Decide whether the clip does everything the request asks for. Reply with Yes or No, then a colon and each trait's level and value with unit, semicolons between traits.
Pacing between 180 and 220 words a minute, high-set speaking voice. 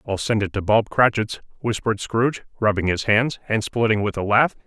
No: fast, 205 wpm; low, 110 Hz